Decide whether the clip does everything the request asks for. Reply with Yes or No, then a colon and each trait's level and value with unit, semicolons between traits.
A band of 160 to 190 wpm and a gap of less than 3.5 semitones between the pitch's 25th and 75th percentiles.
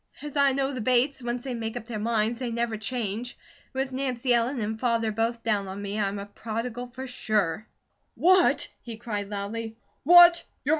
Yes: average, 185 wpm; average, 2.9 semitones